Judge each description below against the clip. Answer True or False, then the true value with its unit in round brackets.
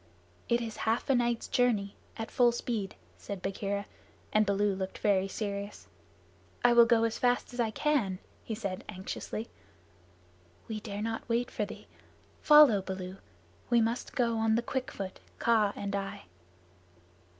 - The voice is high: True (220 Hz)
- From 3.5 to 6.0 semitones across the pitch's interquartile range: False (3.0 semitones)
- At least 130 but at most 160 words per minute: True (155 wpm)